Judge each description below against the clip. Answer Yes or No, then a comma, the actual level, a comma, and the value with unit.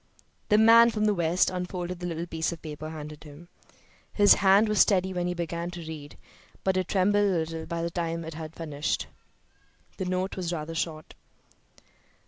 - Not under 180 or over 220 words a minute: Yes, average, 185 wpm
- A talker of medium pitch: Yes, medium, 175 Hz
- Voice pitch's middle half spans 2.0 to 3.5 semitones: Yes, average, 2.7 semitones